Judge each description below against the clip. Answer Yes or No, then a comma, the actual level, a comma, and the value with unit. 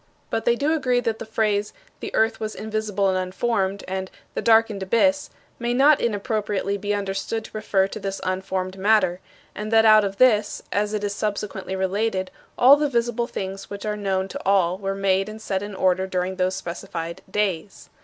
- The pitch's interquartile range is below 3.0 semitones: Yes, narrow, 2.6 semitones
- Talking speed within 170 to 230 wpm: Yes, average, 190 wpm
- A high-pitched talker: Yes, high, 205 Hz